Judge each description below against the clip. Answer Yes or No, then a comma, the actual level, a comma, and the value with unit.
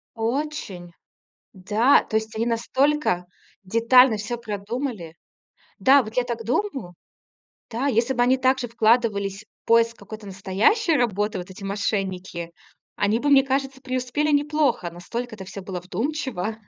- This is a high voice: Yes, high, 230 Hz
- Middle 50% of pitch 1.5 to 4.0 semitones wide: No, average, 4.7 semitones